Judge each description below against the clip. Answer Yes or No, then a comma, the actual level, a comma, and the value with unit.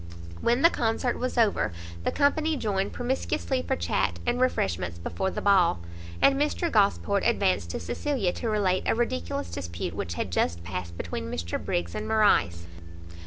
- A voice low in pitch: No, medium, 185 Hz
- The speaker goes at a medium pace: Yes, average, 165 wpm